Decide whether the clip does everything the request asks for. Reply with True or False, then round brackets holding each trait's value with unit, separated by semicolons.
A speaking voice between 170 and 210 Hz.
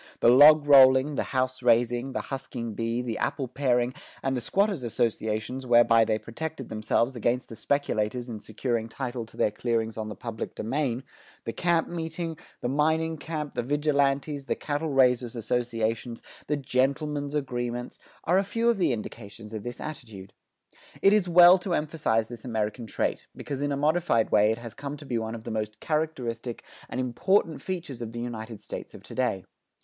False (125 Hz)